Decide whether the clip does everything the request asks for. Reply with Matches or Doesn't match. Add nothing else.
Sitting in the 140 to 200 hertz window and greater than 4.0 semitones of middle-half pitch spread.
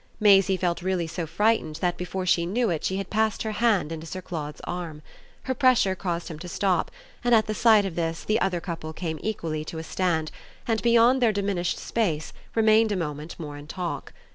Matches